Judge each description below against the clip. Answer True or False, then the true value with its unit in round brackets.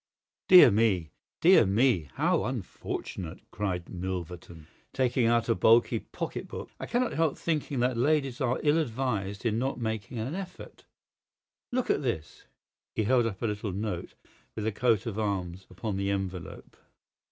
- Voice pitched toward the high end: False (110 Hz)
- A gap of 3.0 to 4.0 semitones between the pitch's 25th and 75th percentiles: False (5.0 semitones)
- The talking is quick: False (155 wpm)